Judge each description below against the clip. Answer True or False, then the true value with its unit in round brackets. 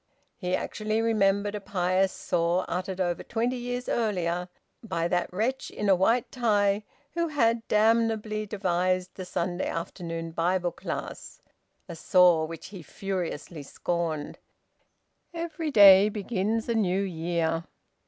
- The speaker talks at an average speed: False (130 wpm)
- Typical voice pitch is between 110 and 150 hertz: False (190 Hz)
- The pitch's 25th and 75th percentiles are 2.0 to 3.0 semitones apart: False (3.8 semitones)